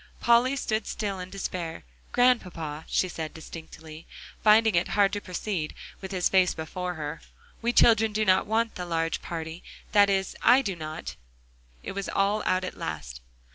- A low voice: No, medium, 185 Hz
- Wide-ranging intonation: No, average, 4.5 semitones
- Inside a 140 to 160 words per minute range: No, average, 170 wpm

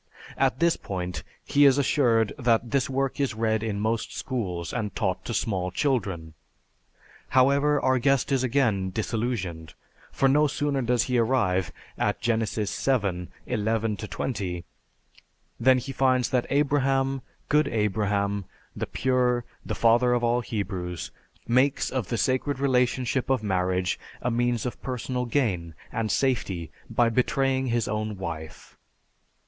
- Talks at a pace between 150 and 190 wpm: No, average, 140 wpm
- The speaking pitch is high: No, low, 120 Hz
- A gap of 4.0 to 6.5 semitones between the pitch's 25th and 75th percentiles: Yes, average, 4.3 semitones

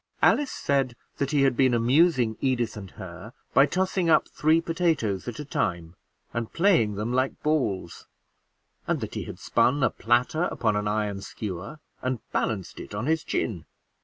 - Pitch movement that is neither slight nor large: No, wide, 6.2 semitones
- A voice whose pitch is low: Yes, low, 125 Hz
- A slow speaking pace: No, average, 170 wpm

